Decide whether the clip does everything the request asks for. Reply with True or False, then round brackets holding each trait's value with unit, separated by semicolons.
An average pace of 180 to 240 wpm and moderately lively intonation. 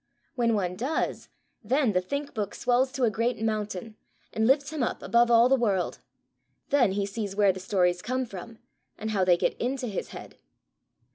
True (190 wpm; 4.0 semitones)